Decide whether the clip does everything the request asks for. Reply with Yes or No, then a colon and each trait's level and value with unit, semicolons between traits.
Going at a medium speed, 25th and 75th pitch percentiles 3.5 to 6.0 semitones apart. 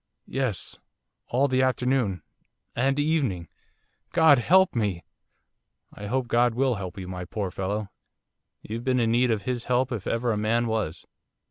Yes: average, 150 wpm; average, 4.0 semitones